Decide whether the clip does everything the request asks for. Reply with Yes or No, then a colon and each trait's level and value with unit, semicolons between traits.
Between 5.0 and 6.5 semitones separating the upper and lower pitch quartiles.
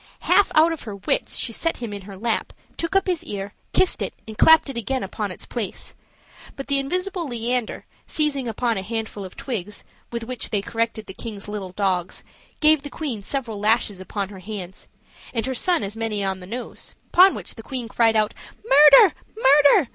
Yes: wide, 5.4 semitones